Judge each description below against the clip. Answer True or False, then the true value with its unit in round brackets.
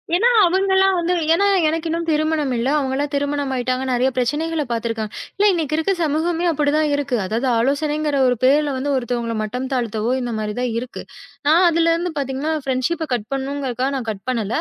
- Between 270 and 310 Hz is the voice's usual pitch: True (280 Hz)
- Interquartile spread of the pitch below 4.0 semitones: False (4.3 semitones)